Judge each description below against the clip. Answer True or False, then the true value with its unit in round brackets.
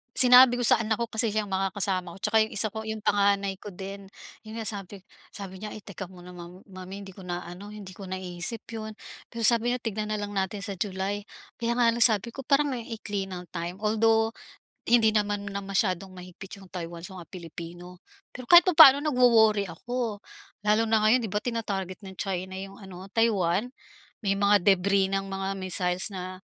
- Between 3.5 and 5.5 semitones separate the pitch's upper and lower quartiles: False (2.8 semitones)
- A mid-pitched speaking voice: False (200 Hz)